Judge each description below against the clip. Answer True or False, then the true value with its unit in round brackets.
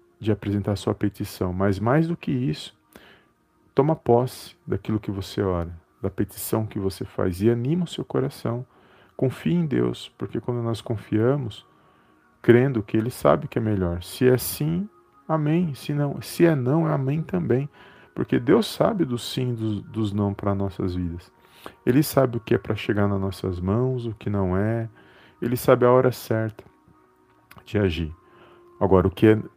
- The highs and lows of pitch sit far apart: False (4.5 semitones)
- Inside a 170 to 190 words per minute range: True (180 wpm)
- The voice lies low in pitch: True (110 Hz)